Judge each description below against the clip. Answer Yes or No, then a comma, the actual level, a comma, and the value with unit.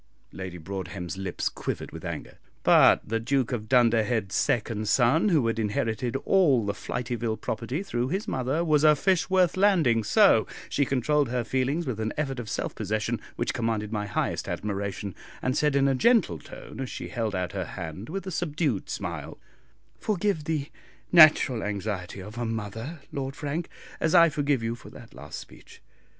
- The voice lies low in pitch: Yes, low, 120 Hz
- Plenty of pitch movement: Yes, wide, 6.0 semitones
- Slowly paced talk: No, average, 175 wpm